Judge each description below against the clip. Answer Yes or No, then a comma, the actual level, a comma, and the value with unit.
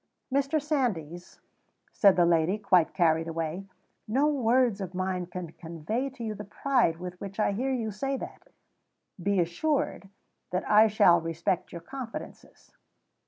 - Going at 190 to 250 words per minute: No, average, 150 wpm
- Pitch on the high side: Yes, high, 195 Hz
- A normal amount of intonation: No, wide, 6.4 semitones